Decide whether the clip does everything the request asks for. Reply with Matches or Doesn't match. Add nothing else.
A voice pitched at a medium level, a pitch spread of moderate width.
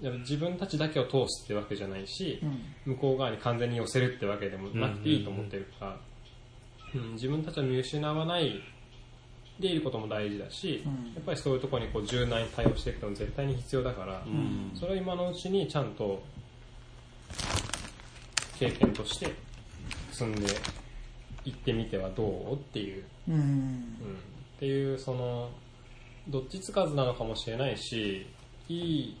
Doesn't match